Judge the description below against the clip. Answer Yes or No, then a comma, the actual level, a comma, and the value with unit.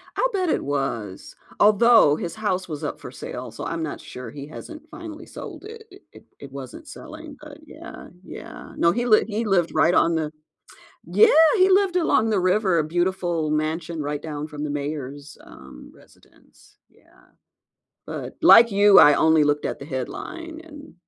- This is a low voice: No, medium, 175 Hz